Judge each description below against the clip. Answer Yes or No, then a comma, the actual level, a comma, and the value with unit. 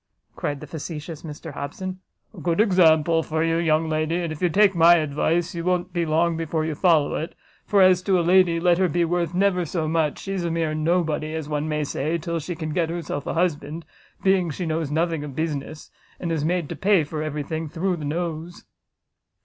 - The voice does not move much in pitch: Yes, narrow, 2.2 semitones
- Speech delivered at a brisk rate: Yes, fast, 215 wpm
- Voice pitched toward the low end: No, medium, 165 Hz